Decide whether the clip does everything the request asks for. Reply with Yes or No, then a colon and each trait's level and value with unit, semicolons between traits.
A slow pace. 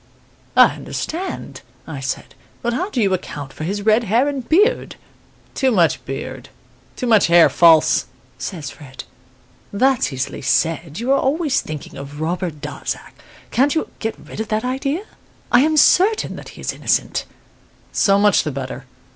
No: average, 165 wpm